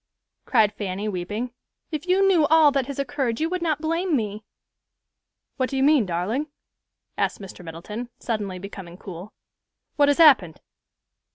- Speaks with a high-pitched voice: Yes, high, 245 Hz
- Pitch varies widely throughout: Yes, wide, 7.2 semitones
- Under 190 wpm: Yes, average, 155 wpm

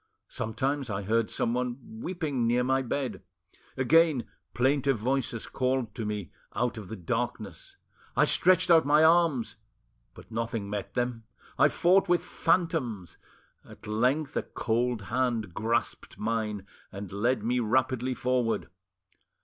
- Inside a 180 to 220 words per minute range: No, slow, 135 wpm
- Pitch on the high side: No, low, 125 Hz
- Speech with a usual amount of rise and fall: Yes, average, 3.5 semitones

